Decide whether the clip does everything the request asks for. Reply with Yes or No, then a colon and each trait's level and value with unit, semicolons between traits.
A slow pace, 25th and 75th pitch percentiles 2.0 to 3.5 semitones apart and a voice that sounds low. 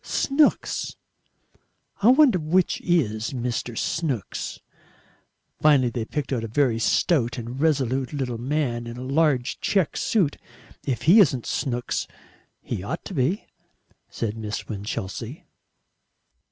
No: slow, 125 wpm; average, 5.2 semitones; low, 130 Hz